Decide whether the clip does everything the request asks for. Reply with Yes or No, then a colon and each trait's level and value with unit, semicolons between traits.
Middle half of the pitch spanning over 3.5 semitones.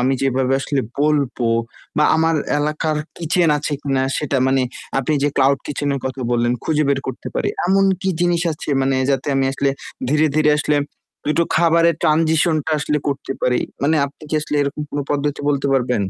No: narrow, 2.6 semitones